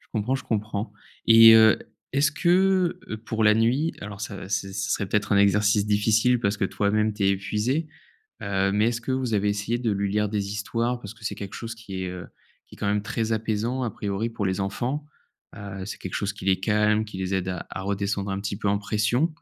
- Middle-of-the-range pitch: No, low, 105 Hz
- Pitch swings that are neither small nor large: No, narrow, 2.3 semitones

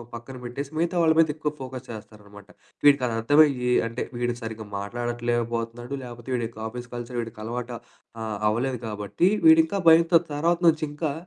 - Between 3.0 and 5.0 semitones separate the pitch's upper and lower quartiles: Yes, average, 4.3 semitones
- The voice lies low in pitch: Yes, low, 120 Hz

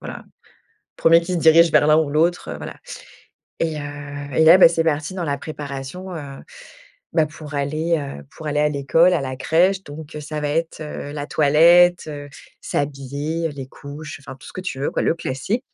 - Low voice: No, medium, 150 Hz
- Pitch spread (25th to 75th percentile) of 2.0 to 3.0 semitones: Yes, narrow, 2.6 semitones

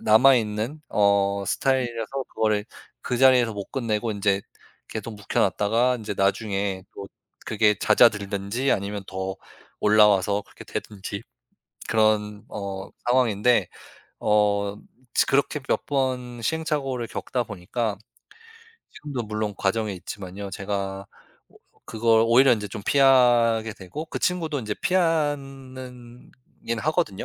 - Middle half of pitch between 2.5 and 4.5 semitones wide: Yes, average, 3.9 semitones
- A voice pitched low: Yes, low, 110 Hz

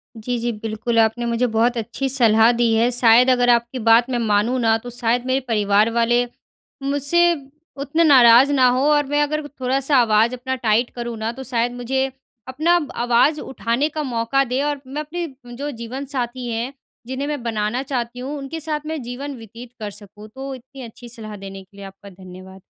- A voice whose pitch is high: Yes, high, 245 Hz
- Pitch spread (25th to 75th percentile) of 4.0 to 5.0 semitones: No, average, 3.0 semitones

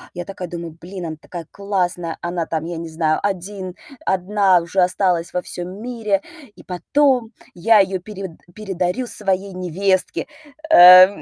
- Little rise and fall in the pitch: Yes, narrow, 2.2 semitones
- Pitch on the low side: No, medium, 185 Hz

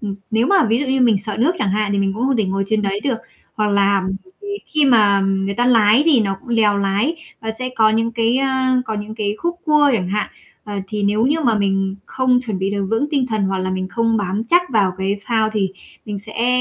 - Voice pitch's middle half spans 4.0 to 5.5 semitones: No, average, 3.6 semitones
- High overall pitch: Yes, high, 215 Hz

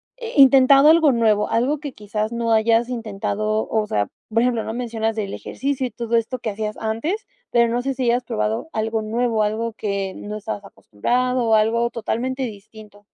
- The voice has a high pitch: Yes, high, 230 Hz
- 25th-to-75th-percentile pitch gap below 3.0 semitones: Yes, narrow, 2.6 semitones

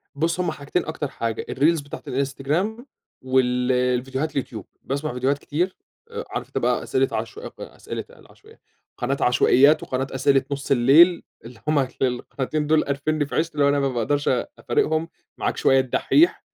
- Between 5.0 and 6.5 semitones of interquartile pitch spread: No, average, 3.2 semitones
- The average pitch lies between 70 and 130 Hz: No, medium, 140 Hz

